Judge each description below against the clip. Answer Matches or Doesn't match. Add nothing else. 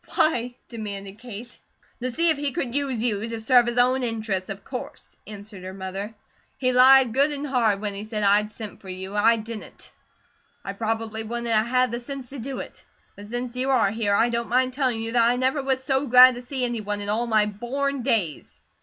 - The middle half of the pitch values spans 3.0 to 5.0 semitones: Matches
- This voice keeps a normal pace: Doesn't match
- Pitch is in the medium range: Doesn't match